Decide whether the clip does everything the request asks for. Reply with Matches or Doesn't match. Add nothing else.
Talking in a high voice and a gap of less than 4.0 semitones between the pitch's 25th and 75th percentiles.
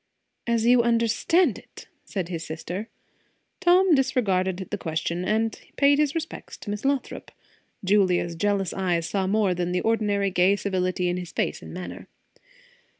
Doesn't match